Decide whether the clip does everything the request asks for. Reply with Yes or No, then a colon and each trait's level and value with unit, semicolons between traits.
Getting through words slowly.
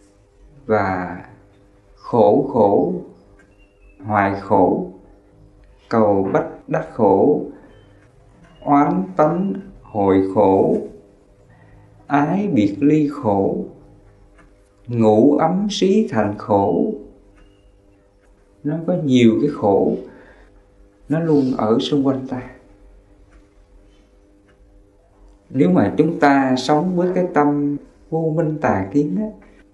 Yes: slow, 95 wpm